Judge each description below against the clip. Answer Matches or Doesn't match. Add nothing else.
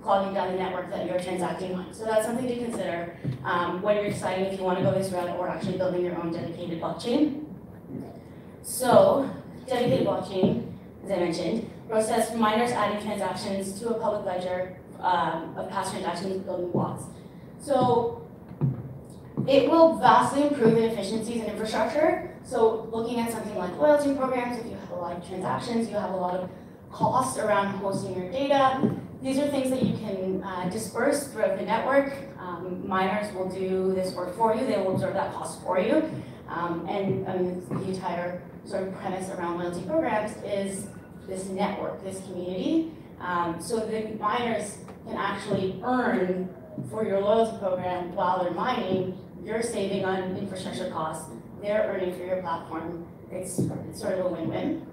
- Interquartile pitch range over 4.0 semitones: Doesn't match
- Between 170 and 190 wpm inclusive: Matches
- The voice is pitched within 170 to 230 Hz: Matches